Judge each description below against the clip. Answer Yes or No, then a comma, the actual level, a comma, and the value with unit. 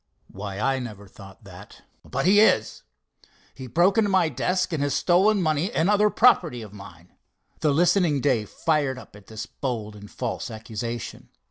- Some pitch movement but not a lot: No, wide, 8.5 semitones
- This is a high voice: No, low, 135 Hz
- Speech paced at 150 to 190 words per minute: Yes, average, 170 wpm